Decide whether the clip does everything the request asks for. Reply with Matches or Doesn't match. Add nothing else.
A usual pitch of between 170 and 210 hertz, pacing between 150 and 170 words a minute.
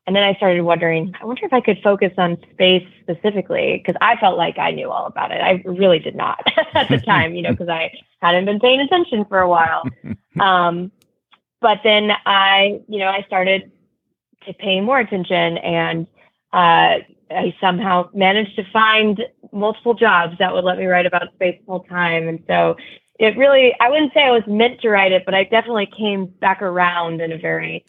Doesn't match